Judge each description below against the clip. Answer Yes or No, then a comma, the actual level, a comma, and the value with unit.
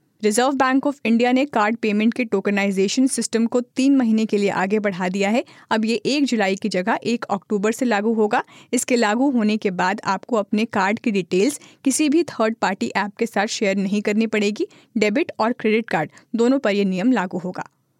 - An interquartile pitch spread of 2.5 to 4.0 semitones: Yes, average, 3.5 semitones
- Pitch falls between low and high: No, high, 220 Hz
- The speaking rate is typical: No, fast, 205 wpm